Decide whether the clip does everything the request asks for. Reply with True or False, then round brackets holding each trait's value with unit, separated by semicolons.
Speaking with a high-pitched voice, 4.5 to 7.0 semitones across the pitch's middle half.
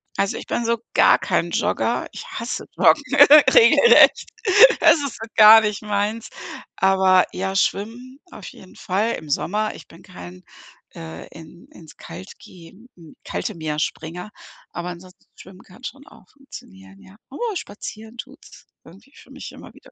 True (195 Hz; 4.9 semitones)